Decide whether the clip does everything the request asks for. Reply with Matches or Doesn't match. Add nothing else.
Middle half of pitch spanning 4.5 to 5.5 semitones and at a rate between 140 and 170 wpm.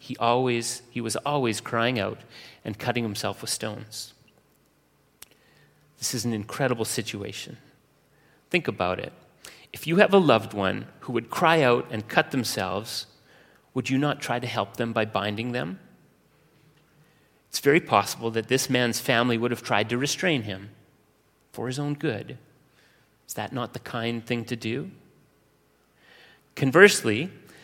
Doesn't match